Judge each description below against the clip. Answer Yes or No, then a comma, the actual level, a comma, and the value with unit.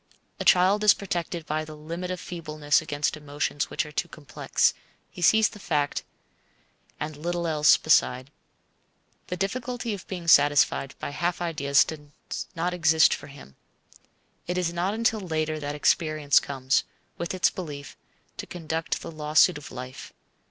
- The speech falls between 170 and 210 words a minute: No, average, 155 wpm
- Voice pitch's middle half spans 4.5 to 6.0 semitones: No, average, 3.3 semitones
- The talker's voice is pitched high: No, medium, 160 Hz